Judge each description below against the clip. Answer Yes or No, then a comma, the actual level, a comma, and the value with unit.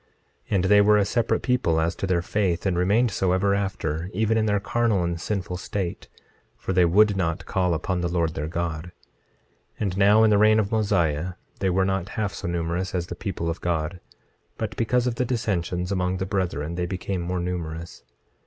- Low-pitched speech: Yes, very low, 95 Hz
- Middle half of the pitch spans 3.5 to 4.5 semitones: No, average, 3.1 semitones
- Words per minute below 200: No, fast, 205 wpm